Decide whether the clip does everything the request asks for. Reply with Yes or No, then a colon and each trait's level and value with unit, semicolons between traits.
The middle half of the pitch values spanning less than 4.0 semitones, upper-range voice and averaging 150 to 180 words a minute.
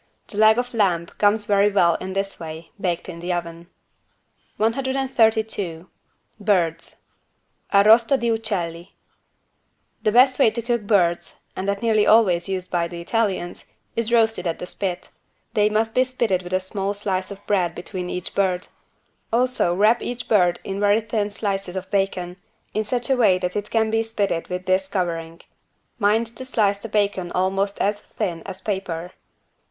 Yes: average, 3.6 semitones; high, 200 Hz; average, 170 wpm